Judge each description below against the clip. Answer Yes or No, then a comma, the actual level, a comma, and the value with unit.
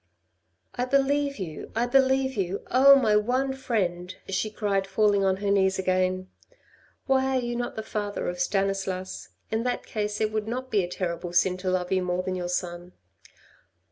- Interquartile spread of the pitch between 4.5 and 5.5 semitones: Yes, average, 4.9 semitones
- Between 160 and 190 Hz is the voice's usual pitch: No, high, 200 Hz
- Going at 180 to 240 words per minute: Yes, average, 190 wpm